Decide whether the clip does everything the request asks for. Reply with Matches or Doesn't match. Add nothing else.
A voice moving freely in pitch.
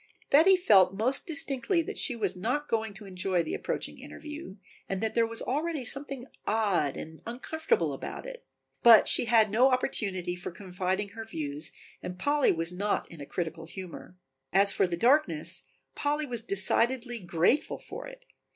Matches